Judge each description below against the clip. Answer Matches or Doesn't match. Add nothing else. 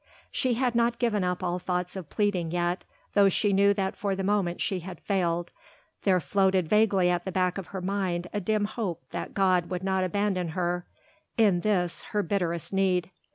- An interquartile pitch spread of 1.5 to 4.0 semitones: Matches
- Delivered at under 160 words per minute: Doesn't match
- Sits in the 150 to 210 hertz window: Matches